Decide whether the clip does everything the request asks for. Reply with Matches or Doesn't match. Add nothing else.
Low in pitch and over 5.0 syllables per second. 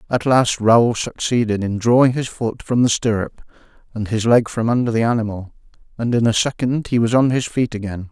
Matches